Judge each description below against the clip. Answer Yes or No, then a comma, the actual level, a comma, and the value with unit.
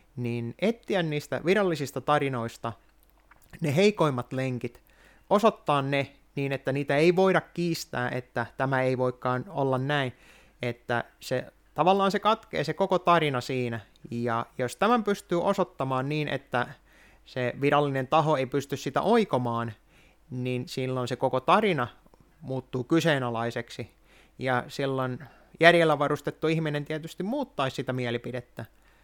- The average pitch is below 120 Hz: No, low, 135 Hz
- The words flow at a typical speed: Yes, average, 125 wpm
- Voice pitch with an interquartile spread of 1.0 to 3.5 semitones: No, average, 4.4 semitones